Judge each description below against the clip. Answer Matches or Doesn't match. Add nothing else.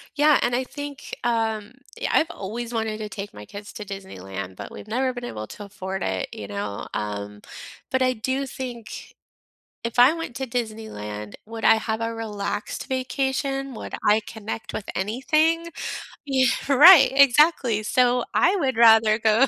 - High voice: Matches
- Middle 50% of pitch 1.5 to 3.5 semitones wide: Doesn't match